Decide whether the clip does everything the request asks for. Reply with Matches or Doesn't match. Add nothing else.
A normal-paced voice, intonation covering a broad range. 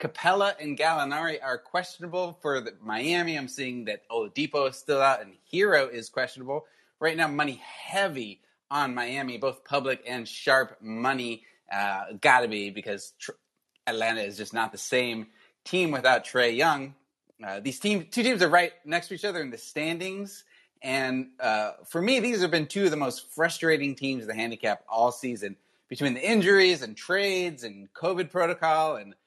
Matches